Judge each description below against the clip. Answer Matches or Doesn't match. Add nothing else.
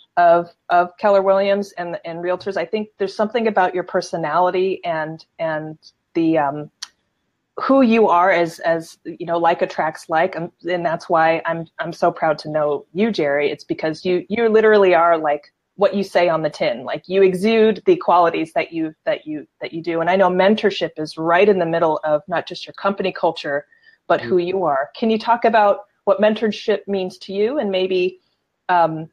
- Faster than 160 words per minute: Matches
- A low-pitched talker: Doesn't match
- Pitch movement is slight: Doesn't match